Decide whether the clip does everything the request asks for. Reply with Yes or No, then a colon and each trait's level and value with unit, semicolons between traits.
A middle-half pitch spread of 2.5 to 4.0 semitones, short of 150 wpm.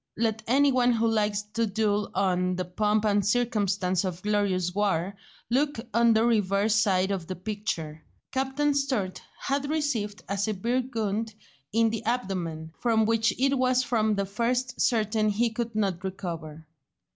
No: average, 3.4 semitones; average, 155 wpm